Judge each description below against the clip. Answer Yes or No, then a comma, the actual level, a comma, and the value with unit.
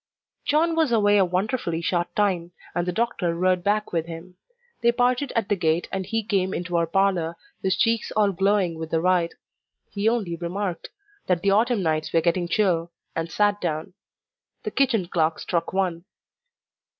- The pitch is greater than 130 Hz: Yes, medium, 185 Hz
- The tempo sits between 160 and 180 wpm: Yes, average, 175 wpm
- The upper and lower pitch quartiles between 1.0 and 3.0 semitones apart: No, average, 3.6 semitones